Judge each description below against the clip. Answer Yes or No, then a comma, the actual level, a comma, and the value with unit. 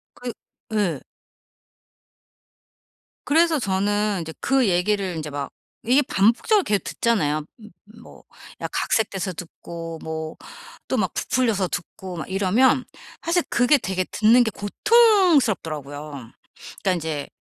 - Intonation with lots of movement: Yes, wide, 6.9 semitones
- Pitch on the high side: Yes, high, 200 Hz